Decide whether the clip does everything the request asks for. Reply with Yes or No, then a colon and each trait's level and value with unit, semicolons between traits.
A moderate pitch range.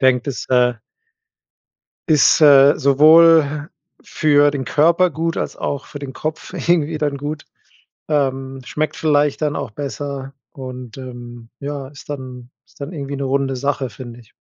No: narrow, 2.3 semitones